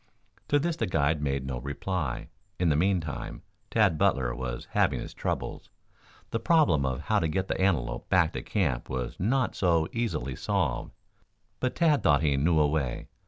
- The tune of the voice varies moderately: No, wide, 6.1 semitones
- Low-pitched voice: Yes, very low, 80 Hz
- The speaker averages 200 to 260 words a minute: No, average, 175 wpm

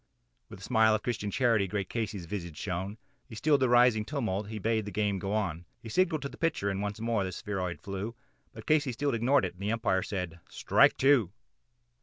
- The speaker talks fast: Yes, fast, 215 wpm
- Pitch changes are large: No, average, 3.7 semitones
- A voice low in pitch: Yes, low, 105 Hz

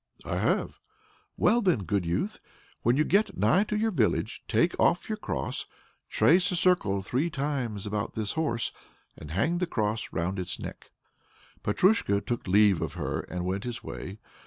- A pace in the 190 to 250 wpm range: No, average, 170 wpm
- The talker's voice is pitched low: Yes, low, 115 Hz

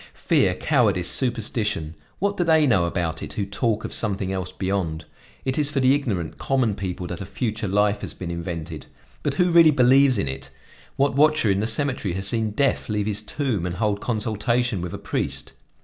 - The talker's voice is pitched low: Yes, low, 105 Hz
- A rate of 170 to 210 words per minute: Yes, average, 195 wpm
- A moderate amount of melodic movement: No, wide, 5.9 semitones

